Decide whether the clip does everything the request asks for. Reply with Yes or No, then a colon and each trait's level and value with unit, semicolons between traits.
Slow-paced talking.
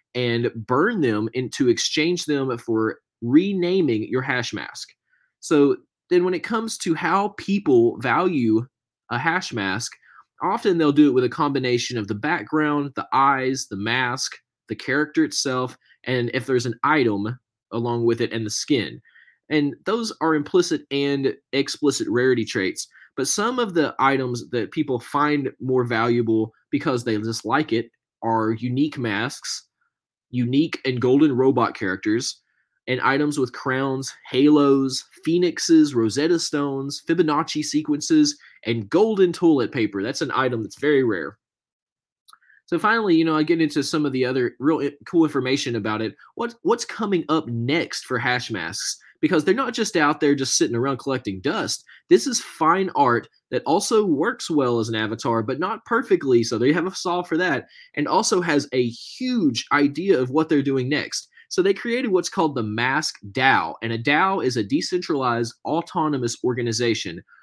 No: average, 165 wpm